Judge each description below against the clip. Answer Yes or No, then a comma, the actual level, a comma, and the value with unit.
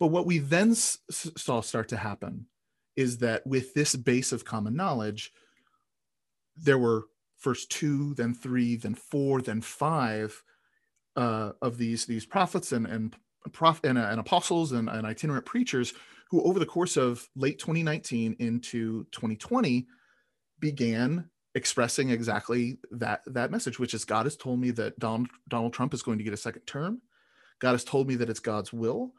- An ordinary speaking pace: Yes, average, 160 wpm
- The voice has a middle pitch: No, low, 125 Hz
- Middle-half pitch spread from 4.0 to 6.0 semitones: Yes, average, 4.8 semitones